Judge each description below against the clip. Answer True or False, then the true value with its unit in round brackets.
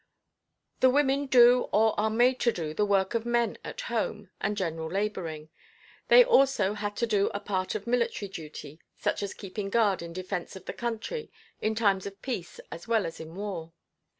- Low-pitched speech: False (205 Hz)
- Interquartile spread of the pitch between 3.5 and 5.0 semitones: True (4.0 semitones)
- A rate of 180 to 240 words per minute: True (190 wpm)